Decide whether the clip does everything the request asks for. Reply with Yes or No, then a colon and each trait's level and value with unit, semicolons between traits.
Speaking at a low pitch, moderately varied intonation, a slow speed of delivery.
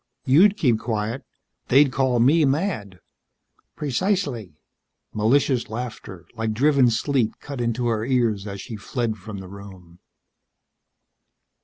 Yes: low, 120 Hz; average, 4.2 semitones; slow, 120 wpm